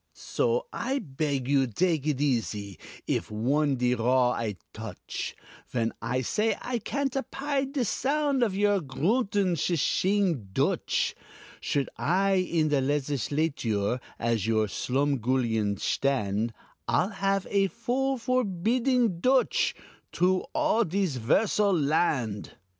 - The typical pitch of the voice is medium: Yes, medium, 160 Hz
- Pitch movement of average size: No, wide, 8.9 semitones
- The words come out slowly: Yes, slow, 125 wpm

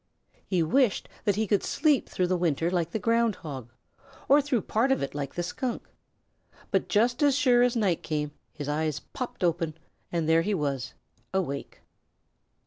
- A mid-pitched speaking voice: Yes, medium, 180 Hz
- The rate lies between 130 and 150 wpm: No, average, 175 wpm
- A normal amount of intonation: No, wide, 7.1 semitones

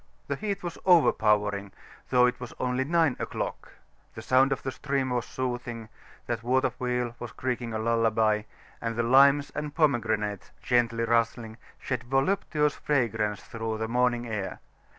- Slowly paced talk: No, average, 150 wpm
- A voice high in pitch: No, low, 120 Hz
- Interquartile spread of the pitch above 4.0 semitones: No, average, 2.8 semitones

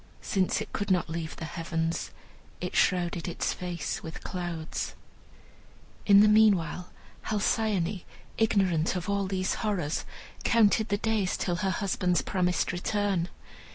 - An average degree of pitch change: Yes, average, 3.1 semitones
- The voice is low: No, medium, 185 Hz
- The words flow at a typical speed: No, slow, 130 wpm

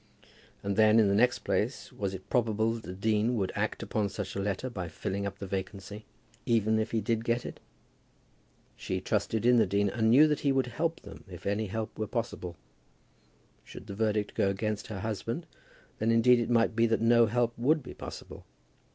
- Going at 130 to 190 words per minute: No, fast, 205 wpm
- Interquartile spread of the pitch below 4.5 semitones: Yes, average, 2.7 semitones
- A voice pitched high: No, low, 110 Hz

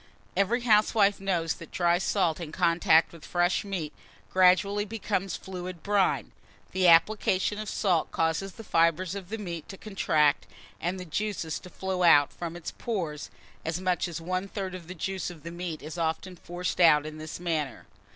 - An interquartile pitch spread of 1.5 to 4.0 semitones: Yes, average, 2.8 semitones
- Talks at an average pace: Yes, average, 180 wpm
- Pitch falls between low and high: Yes, medium, 180 Hz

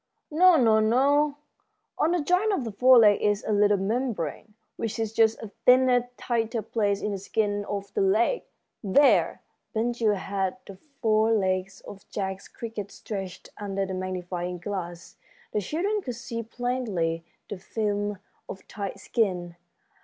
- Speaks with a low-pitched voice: No, high, 210 Hz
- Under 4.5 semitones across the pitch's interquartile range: Yes, average, 3.7 semitones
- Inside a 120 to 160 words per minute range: Yes, average, 155 wpm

